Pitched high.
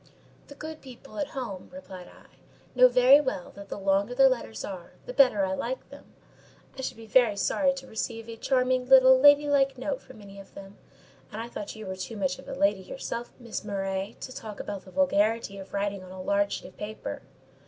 Yes: high, 225 Hz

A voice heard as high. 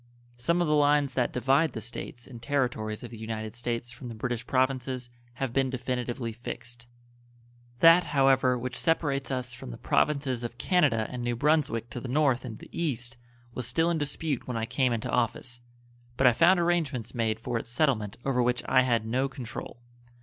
No: low, 125 Hz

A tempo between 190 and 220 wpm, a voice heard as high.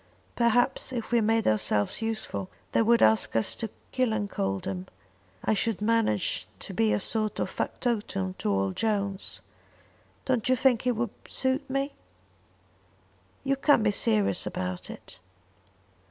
No: average, 140 wpm; high, 220 Hz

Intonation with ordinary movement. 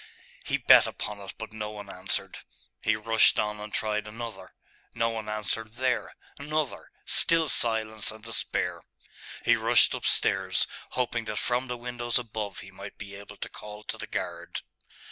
No: narrow, 2.1 semitones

